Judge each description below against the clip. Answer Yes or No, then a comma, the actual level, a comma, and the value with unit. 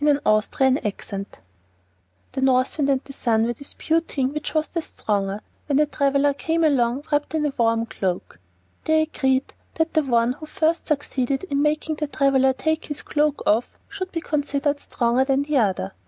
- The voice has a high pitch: Yes, very high, 280 Hz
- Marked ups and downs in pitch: No, average, 3.5 semitones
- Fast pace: No, average, 175 wpm